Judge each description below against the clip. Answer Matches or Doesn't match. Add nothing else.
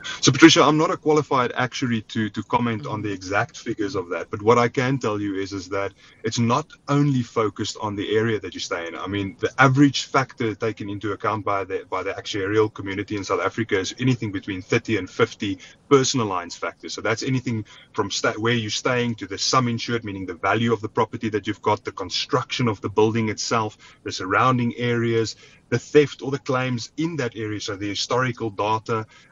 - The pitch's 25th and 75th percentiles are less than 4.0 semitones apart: Matches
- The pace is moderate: Doesn't match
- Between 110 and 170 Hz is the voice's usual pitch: Matches